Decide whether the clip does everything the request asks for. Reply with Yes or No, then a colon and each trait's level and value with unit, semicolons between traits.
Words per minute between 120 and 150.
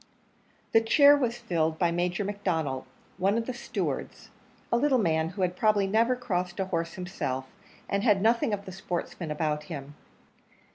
No: average, 170 wpm